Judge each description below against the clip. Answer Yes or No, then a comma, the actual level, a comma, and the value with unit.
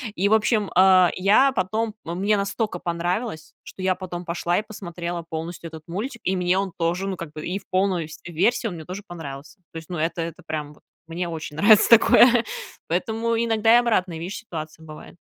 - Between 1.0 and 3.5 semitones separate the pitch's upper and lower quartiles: No, average, 3.9 semitones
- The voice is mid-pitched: Yes, medium, 180 Hz